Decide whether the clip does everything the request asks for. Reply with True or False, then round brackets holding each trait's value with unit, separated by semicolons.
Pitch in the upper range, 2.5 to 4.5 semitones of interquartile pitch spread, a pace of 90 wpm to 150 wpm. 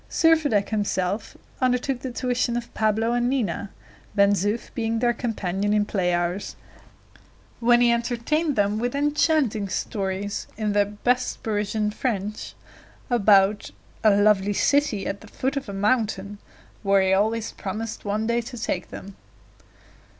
True (215 Hz; 3.1 semitones; 145 wpm)